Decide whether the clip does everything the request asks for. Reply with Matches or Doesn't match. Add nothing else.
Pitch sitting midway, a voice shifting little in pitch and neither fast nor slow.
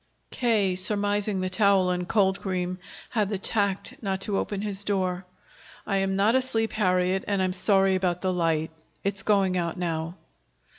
Doesn't match